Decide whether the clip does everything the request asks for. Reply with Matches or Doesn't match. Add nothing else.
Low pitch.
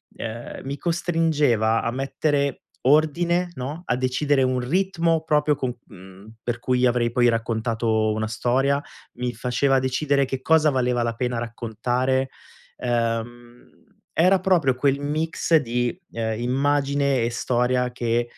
Matches